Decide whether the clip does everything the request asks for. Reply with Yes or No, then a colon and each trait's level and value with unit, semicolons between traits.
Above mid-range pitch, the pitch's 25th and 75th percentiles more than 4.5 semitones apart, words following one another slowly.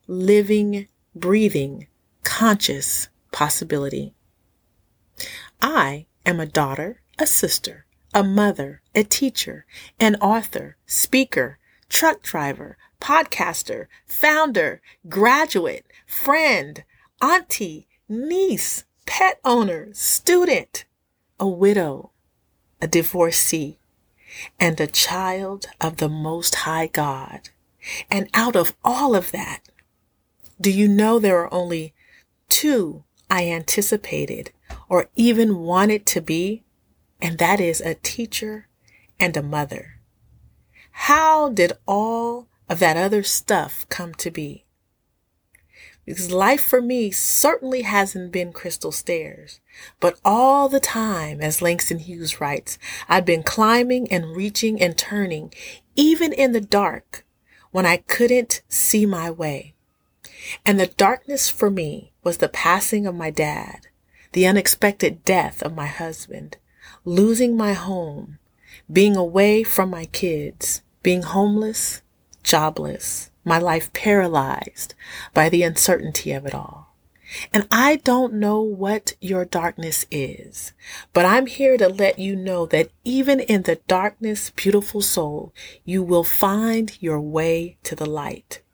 Yes: high, 195 Hz; average, 5.1 semitones; slow, 120 wpm